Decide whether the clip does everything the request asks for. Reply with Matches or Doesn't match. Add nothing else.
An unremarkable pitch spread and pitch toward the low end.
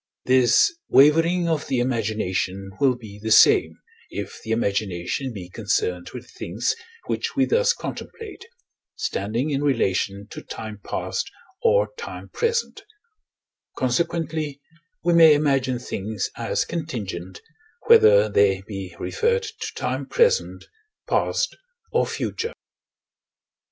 Doesn't match